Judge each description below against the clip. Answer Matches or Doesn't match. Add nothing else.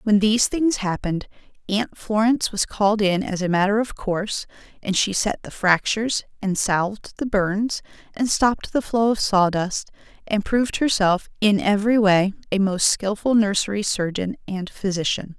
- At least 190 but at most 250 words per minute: Doesn't match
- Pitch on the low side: Doesn't match